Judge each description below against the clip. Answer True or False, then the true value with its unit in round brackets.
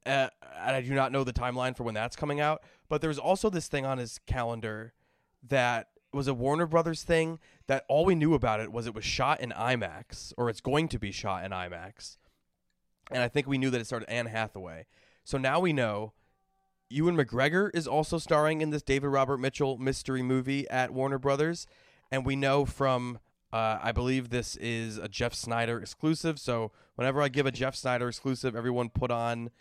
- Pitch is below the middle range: True (130 Hz)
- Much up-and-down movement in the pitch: False (3.7 semitones)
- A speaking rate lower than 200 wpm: False (205 wpm)